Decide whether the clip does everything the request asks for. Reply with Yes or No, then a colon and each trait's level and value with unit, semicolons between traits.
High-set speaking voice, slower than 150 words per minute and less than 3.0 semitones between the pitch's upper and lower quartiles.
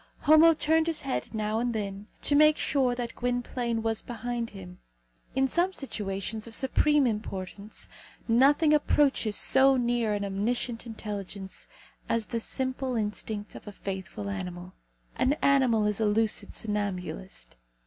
No: high, 230 Hz; average, 140 wpm; average, 4.3 semitones